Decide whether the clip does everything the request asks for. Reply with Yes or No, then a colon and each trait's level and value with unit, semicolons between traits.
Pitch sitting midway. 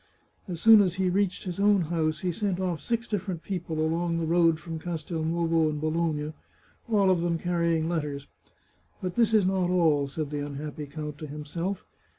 Yes: medium, 170 Hz